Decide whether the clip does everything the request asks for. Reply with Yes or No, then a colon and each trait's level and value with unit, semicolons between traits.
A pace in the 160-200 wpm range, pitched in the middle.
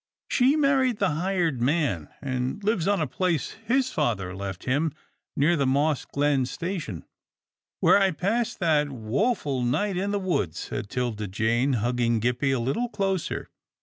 Yes: average, 165 wpm; medium, 145 Hz